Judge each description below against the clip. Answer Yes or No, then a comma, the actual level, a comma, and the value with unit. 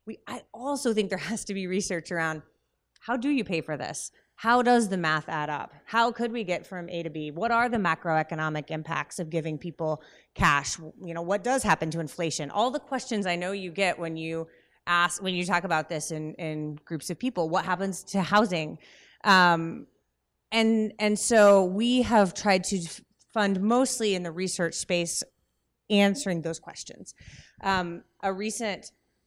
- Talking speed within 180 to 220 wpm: Yes, average, 185 wpm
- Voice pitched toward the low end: No, medium, 180 Hz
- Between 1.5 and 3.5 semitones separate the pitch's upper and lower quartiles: No, average, 4.4 semitones